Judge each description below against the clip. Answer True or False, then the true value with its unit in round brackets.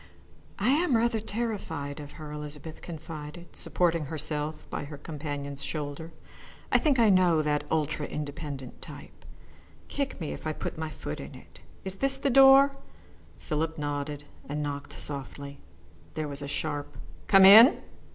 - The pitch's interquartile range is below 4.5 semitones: False (4.8 semitones)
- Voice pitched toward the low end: False (155 Hz)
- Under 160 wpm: True (150 wpm)